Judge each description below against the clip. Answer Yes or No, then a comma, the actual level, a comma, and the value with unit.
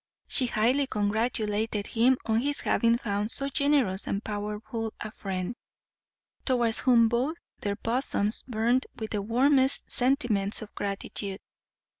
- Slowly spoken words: Yes, slow, 130 wpm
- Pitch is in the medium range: No, high, 225 Hz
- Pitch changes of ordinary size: Yes, average, 3.5 semitones